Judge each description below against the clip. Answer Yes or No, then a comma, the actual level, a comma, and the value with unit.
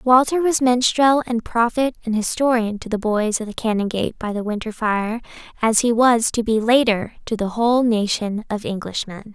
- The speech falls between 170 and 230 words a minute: Yes, average, 185 wpm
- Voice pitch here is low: No, high, 225 Hz